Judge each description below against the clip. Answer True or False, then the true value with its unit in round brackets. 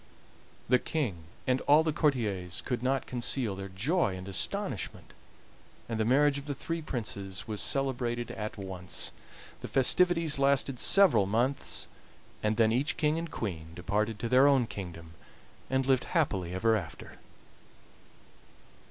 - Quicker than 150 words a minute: False (145 wpm)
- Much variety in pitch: True (5.9 semitones)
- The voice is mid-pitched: False (120 Hz)